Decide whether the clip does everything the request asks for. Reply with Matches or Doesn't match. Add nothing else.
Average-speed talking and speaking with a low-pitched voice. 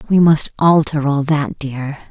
Doesn't match